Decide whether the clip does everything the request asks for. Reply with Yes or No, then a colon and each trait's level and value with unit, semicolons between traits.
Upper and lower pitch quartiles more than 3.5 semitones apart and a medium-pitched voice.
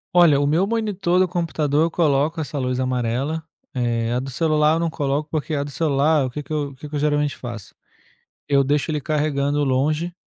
No: narrow, 2.6 semitones; medium, 145 Hz